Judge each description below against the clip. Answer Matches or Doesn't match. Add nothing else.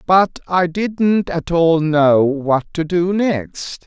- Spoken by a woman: Doesn't match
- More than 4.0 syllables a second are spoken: Doesn't match